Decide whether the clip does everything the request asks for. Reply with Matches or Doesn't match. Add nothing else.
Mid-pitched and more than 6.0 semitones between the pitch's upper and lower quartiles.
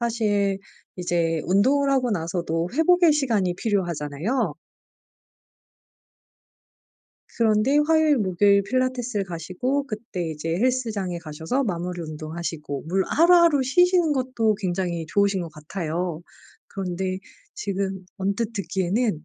Doesn't match